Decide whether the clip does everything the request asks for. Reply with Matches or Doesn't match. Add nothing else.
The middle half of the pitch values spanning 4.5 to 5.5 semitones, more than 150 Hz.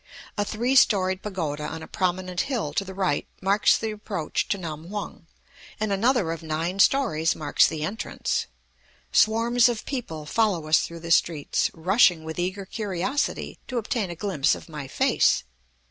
Matches